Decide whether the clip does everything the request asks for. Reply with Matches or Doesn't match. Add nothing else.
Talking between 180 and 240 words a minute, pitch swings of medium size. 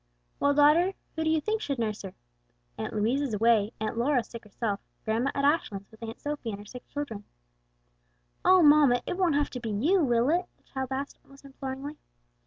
Matches